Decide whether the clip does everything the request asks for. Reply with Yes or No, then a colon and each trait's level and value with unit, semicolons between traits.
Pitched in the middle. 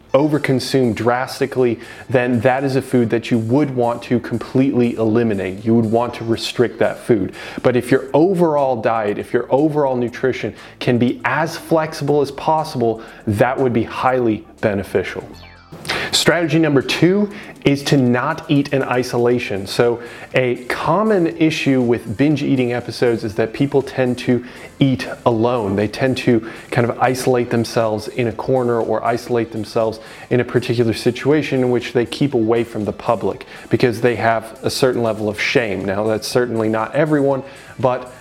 No: low, 125 Hz